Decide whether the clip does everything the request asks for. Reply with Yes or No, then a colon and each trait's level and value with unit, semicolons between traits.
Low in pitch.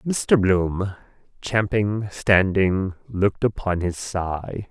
Yes: low, 100 Hz